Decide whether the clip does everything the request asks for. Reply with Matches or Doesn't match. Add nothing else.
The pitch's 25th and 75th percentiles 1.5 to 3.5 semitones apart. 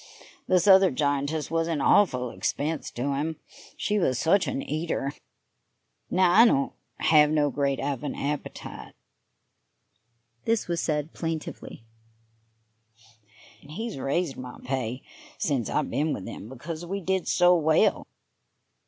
Doesn't match